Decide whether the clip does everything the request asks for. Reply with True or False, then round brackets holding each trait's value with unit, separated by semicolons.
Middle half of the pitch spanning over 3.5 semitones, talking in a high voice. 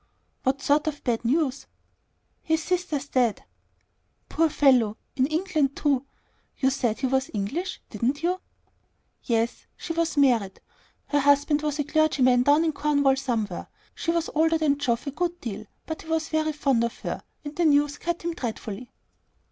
True (3.9 semitones; 285 Hz)